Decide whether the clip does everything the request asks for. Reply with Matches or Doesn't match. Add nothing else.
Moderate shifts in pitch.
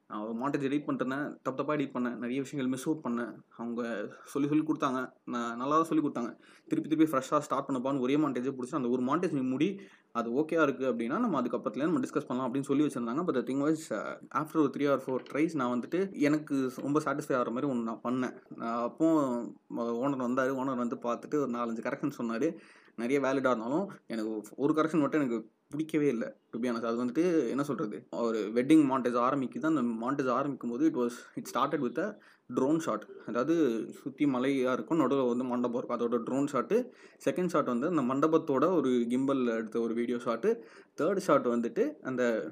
Matches